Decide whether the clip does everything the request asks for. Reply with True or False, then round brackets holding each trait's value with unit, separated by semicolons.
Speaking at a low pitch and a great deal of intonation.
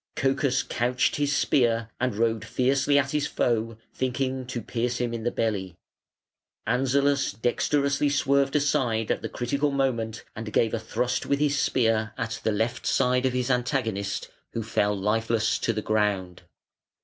False (120 Hz; 3.3 semitones)